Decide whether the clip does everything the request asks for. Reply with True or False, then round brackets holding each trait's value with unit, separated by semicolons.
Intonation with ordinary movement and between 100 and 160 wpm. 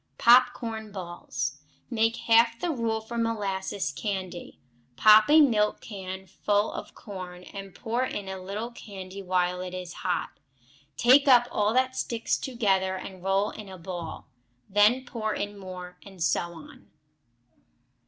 True (3.6 semitones; 150 wpm)